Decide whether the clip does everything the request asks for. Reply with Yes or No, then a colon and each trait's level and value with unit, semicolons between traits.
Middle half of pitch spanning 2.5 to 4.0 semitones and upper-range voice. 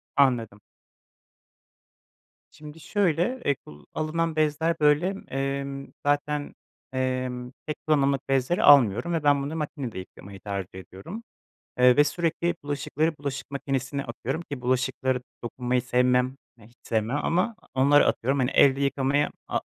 No: average, 3.1 semitones; medium, 140 Hz